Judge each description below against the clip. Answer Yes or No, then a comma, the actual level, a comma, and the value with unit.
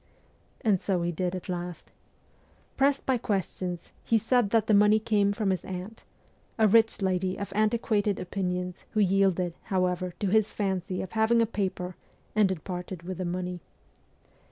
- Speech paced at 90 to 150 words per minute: No, average, 165 wpm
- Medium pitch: No, high, 195 Hz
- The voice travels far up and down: No, average, 3.0 semitones